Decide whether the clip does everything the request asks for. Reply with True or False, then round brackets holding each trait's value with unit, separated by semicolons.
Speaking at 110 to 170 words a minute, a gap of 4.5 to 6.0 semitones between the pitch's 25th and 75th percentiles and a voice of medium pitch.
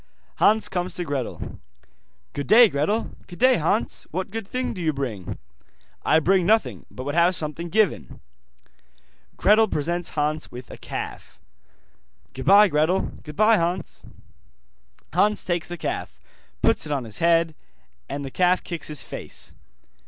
True (145 wpm; 5.0 semitones; 170 Hz)